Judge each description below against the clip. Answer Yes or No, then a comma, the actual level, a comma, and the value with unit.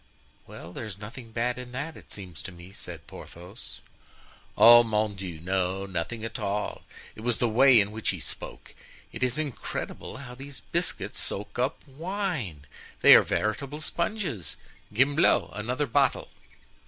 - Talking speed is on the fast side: No, average, 155 wpm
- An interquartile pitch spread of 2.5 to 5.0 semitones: No, wide, 5.5 semitones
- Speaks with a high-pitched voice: No, low, 115 Hz